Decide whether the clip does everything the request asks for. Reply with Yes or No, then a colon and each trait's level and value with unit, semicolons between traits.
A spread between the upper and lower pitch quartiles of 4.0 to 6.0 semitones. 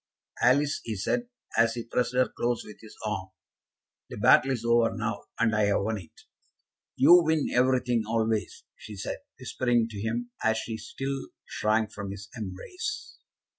No: average, 2.8 semitones